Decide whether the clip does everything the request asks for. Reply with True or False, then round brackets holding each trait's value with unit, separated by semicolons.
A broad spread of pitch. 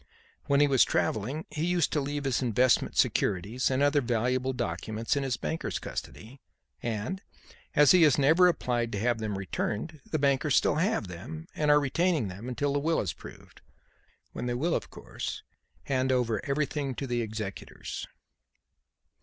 False (4.3 semitones)